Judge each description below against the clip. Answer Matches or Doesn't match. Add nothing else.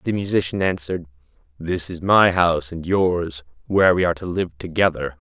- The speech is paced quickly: Doesn't match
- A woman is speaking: Doesn't match